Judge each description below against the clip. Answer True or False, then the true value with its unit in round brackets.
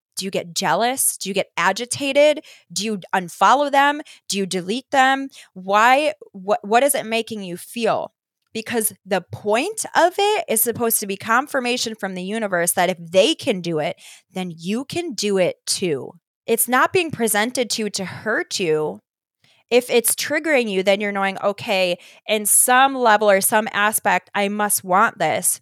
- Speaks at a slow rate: False (180 wpm)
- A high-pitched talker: True (215 Hz)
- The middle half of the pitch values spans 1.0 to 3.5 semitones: False (4.9 semitones)